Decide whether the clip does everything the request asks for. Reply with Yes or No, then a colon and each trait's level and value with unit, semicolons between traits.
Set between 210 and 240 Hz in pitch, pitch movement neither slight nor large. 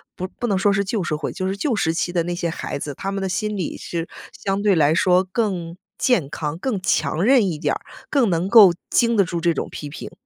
No: medium, 185 Hz; average, 3.5 semitones